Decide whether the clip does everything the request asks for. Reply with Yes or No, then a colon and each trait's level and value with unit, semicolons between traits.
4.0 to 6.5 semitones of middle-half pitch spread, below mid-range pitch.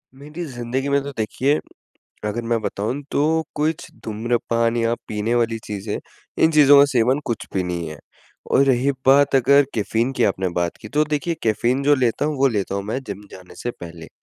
Yes: average, 4.7 semitones; low, 120 Hz